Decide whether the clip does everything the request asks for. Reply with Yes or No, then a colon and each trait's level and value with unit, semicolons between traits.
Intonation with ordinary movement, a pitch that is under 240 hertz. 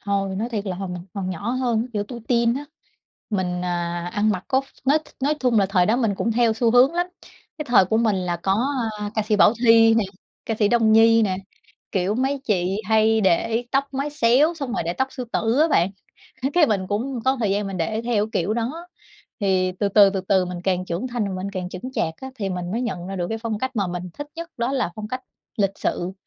Yes: average, 4.4 semitones; high, 215 Hz